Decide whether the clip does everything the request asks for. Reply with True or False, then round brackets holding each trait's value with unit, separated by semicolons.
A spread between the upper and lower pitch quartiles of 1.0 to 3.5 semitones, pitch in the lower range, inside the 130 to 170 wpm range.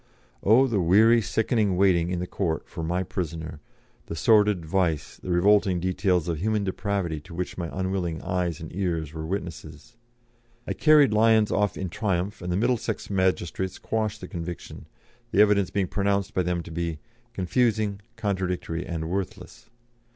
True (3.2 semitones; 95 Hz; 160 wpm)